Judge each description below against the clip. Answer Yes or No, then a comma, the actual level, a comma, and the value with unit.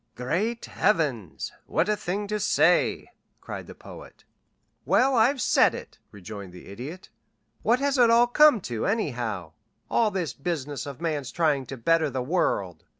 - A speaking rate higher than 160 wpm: No, average, 155 wpm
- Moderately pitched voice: Yes, medium, 165 Hz